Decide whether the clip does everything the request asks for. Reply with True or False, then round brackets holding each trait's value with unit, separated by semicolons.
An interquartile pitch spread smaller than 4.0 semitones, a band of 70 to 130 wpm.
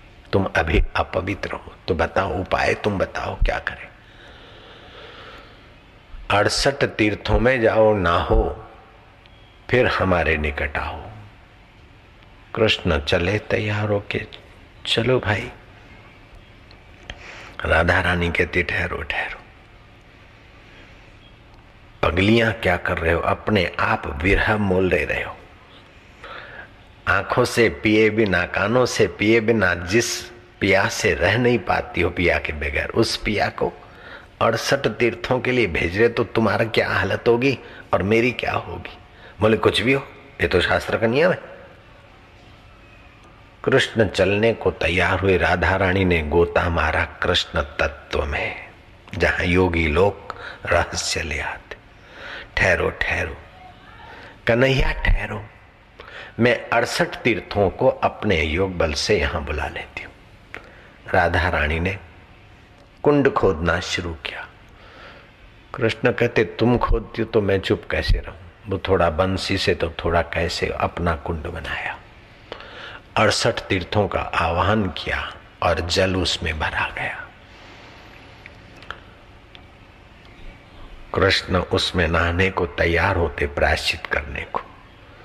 True (3.5 semitones; 120 wpm)